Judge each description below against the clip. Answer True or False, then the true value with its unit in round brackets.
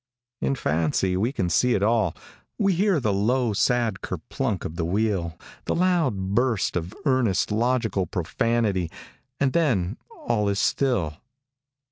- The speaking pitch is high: False (105 Hz)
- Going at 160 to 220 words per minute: False (140 wpm)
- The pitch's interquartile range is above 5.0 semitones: True (5.4 semitones)